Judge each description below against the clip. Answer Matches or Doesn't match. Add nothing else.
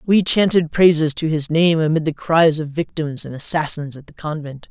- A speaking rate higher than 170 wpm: Matches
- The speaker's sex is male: Doesn't match